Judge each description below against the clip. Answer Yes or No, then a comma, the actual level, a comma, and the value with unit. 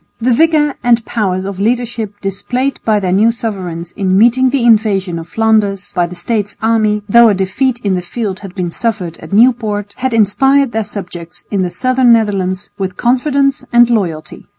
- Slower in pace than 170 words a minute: No, average, 180 wpm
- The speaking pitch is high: Yes, high, 215 Hz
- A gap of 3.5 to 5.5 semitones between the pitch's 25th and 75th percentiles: Yes, average, 3.9 semitones